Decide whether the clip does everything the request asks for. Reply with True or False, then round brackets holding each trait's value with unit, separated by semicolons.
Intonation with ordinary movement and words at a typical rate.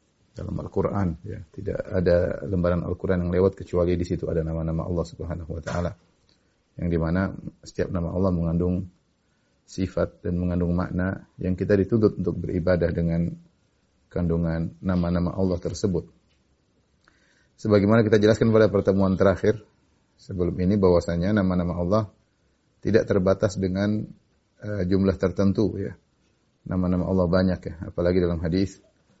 False (2.1 semitones; 130 wpm)